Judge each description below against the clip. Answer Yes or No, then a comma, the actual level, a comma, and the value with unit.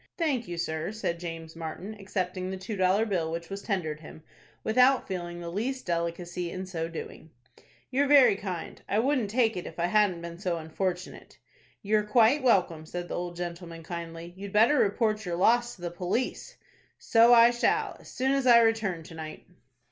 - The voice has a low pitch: No, medium, 185 Hz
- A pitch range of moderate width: Yes, average, 4.9 semitones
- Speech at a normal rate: Yes, average, 185 wpm